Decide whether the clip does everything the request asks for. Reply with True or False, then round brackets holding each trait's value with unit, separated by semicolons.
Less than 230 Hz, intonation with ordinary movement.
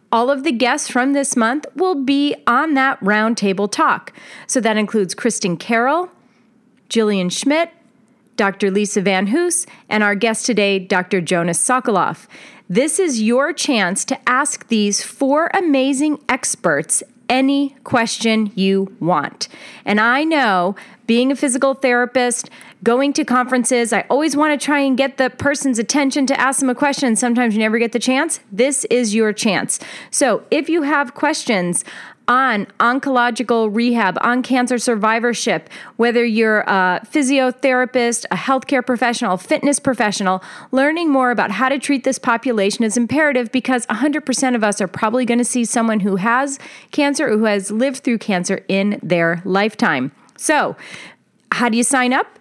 False (245 Hz; 3.9 semitones)